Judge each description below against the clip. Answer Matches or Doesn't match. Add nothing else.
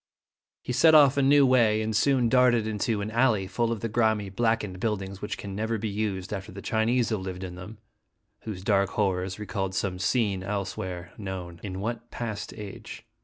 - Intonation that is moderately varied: Matches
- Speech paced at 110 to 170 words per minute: Doesn't match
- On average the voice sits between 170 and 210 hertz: Doesn't match